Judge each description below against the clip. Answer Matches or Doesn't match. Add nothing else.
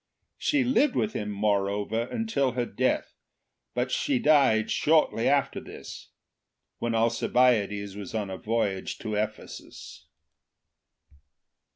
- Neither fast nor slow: Doesn't match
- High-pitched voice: Doesn't match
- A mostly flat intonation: Doesn't match